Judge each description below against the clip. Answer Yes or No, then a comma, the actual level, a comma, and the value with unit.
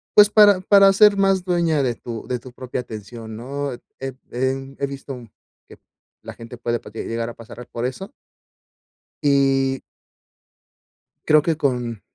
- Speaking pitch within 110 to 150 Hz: Yes, low, 135 Hz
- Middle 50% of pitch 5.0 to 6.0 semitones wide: Yes, wide, 5.5 semitones